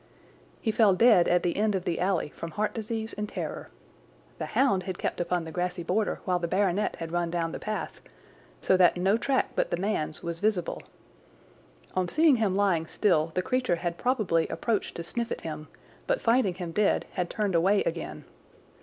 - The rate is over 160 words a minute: Yes, average, 195 wpm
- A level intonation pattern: No, average, 3.8 semitones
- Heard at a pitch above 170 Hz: Yes, medium, 185 Hz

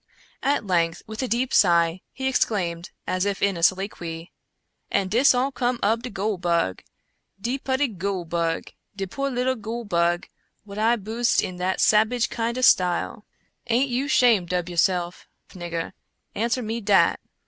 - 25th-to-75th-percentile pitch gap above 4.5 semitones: Yes, average, 5.3 semitones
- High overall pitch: Yes, high, 205 Hz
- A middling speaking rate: Yes, average, 170 wpm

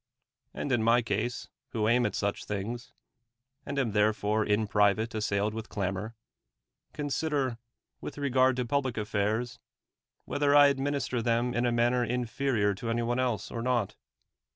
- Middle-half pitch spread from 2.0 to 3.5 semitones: Yes, average, 3.0 semitones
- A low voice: Yes, low, 120 Hz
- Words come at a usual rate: Yes, average, 160 wpm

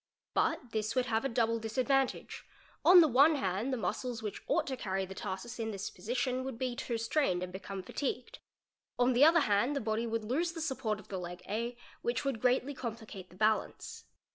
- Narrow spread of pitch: No, average, 3.6 semitones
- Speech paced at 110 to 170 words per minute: No, fast, 205 wpm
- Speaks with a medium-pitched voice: No, high, 235 Hz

